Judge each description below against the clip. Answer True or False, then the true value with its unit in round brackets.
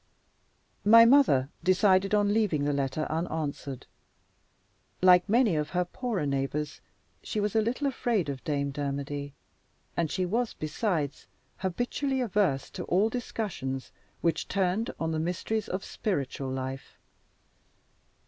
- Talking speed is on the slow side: True (130 wpm)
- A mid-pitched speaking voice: True (180 Hz)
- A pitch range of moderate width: False (6.9 semitones)